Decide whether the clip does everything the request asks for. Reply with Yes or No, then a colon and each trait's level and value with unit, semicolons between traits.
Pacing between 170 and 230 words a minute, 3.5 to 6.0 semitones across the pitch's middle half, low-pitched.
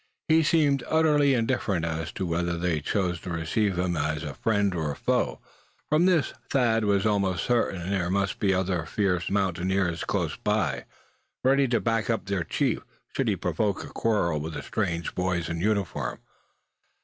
Yes: average, 180 wpm; average, 4.7 semitones; very low, 95 Hz